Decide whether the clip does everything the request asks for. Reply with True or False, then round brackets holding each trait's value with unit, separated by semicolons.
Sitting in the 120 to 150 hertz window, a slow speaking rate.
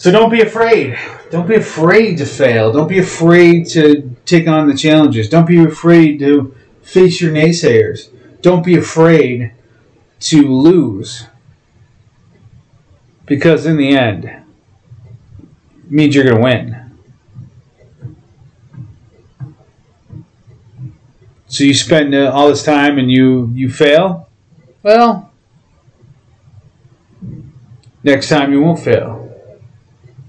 True (140 Hz; 110 wpm)